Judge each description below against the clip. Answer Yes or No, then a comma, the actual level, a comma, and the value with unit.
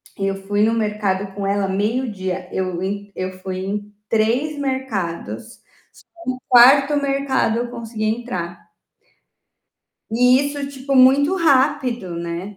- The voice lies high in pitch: Yes, high, 220 Hz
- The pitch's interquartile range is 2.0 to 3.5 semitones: No, average, 5.3 semitones